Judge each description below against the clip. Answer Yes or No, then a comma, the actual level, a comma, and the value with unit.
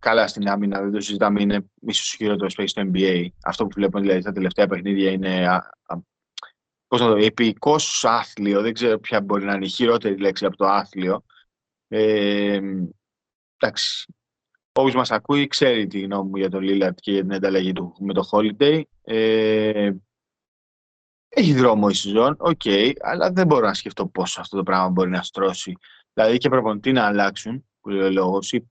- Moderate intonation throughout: No, narrow, 2.3 semitones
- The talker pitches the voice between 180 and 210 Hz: No, low, 100 Hz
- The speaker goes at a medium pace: No, fast, 180 wpm